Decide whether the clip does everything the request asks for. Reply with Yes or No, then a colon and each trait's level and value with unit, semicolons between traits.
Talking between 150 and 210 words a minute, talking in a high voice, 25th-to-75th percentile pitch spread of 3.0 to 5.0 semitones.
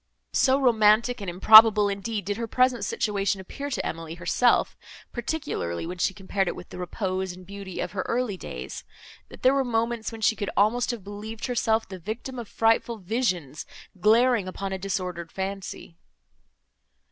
Yes: average, 170 wpm; high, 205 Hz; average, 3.9 semitones